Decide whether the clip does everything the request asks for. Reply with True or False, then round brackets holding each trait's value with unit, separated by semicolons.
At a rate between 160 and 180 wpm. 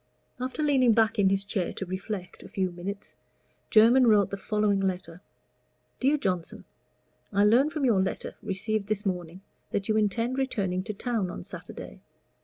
True (165 wpm)